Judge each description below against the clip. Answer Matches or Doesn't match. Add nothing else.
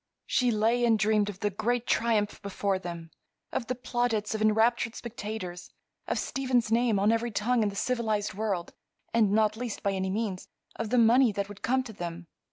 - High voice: Matches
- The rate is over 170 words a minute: Matches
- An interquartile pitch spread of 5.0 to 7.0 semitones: Doesn't match